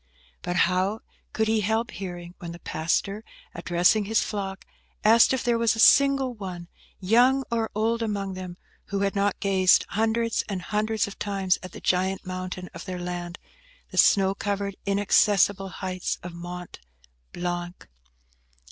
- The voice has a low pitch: No, high, 195 Hz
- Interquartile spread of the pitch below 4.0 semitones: Yes, average, 3.2 semitones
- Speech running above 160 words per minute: No, average, 150 wpm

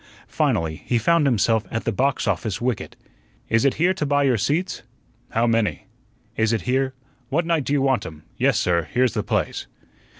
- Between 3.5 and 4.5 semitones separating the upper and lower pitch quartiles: Yes, average, 4.0 semitones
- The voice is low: Yes, low, 125 Hz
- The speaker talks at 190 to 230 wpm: Yes, average, 195 wpm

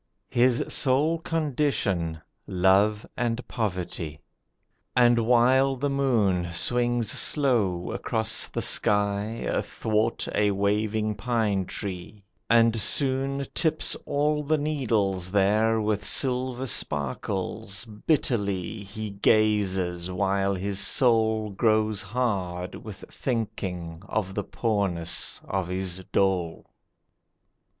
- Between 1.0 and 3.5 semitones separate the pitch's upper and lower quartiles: No, average, 4.0 semitones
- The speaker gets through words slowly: Yes, slow, 100 wpm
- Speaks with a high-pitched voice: No, low, 105 Hz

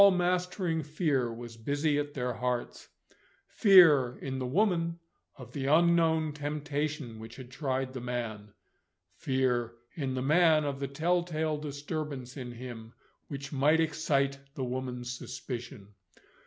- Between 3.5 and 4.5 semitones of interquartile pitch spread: Yes, average, 3.9 semitones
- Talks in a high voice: No, medium, 140 Hz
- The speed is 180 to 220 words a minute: No, average, 140 wpm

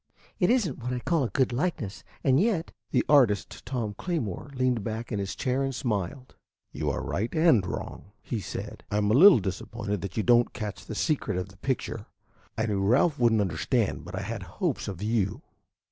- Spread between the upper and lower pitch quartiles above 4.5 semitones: Yes, average, 5.0 semitones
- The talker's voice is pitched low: Yes, low, 115 Hz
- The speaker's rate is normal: No, fast, 210 wpm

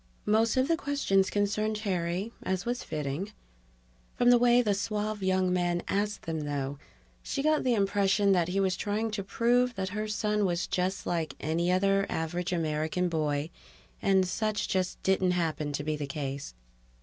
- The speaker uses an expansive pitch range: No, average, 3.8 semitones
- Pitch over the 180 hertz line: Yes, high, 190 Hz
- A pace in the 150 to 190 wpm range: Yes, average, 175 wpm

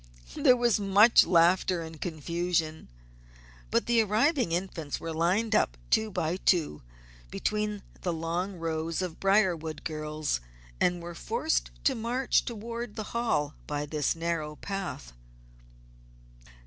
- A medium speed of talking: No, slow, 125 wpm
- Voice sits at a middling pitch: Yes, medium, 175 Hz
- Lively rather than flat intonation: No, average, 4.9 semitones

